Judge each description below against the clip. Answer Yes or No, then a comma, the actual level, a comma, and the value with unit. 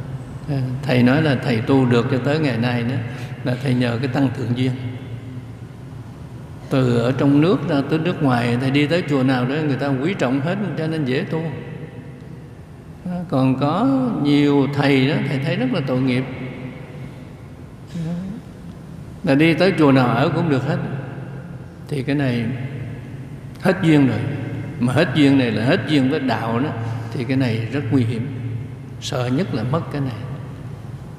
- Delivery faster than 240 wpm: No, average, 170 wpm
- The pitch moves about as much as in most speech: No, narrow, 2.2 semitones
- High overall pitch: No, low, 135 Hz